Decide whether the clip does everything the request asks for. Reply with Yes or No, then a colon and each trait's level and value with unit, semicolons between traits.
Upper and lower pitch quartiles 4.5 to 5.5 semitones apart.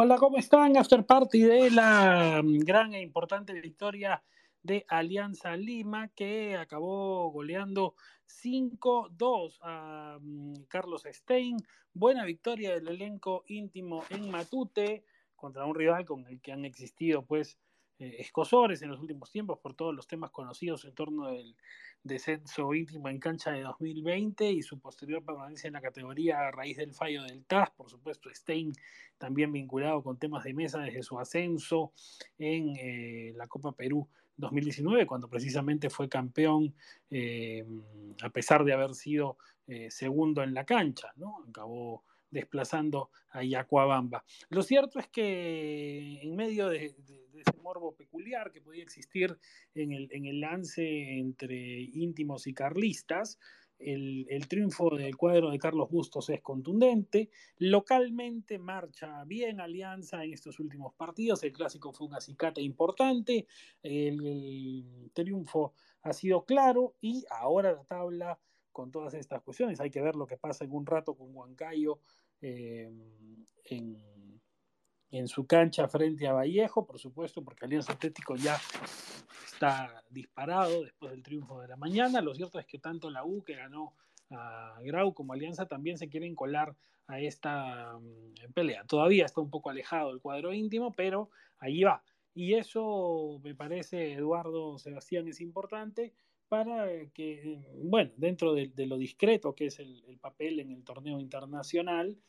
Yes: average, 5.0 semitones